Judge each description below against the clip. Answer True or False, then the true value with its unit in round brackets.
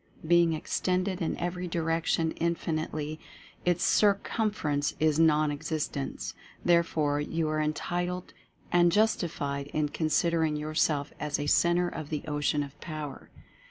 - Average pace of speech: False (125 wpm)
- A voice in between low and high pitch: True (160 Hz)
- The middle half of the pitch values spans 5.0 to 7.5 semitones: False (2.5 semitones)